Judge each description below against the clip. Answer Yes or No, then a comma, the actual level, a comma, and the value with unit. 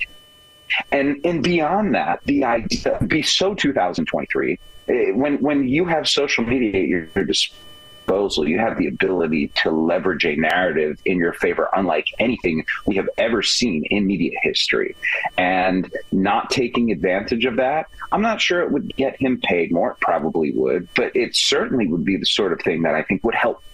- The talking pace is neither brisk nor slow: Yes, average, 180 wpm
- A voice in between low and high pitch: Yes, medium, 145 Hz